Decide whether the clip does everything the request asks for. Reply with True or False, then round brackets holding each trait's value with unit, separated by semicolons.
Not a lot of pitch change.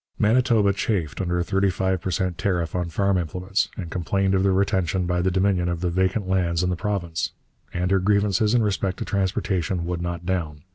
True (2.1 semitones)